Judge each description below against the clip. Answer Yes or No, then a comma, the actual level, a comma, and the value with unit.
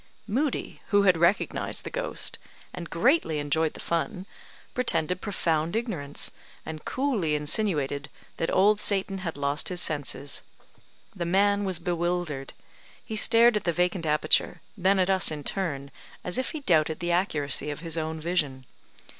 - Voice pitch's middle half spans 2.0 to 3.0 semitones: No, average, 4.6 semitones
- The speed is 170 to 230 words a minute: No, average, 155 wpm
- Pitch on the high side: No, medium, 175 Hz